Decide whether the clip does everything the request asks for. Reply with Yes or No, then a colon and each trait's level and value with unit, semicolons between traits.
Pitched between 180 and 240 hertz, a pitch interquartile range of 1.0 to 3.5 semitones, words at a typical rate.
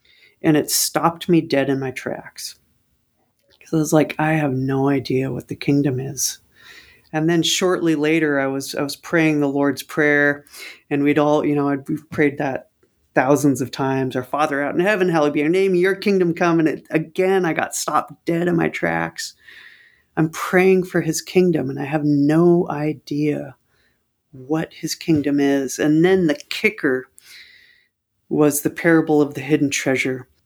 No: medium, 150 Hz; average, 2.9 semitones; average, 180 wpm